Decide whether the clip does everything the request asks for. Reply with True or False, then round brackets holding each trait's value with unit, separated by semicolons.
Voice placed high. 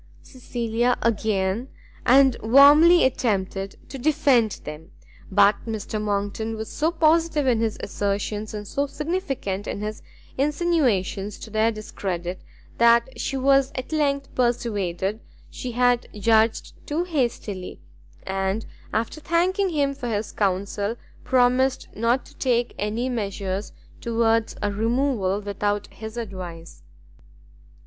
True (230 Hz)